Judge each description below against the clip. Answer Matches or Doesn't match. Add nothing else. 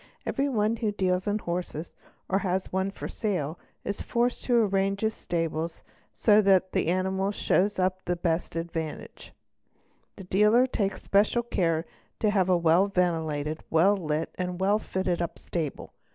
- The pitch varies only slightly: Doesn't match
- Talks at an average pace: Matches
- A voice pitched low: Doesn't match